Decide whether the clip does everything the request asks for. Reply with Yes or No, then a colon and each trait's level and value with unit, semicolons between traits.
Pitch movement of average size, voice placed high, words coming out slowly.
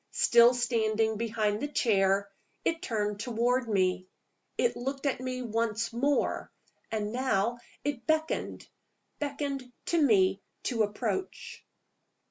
Yes: average, 3.9 semitones; high, 235 Hz; slow, 115 wpm